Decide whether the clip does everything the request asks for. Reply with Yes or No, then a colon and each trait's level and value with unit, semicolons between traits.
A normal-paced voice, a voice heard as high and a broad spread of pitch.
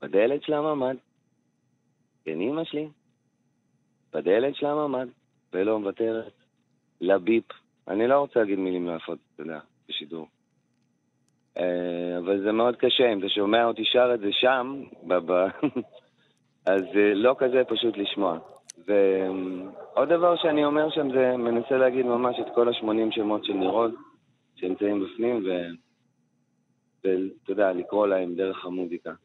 No: average, 130 wpm; low, 110 Hz; wide, 5.7 semitones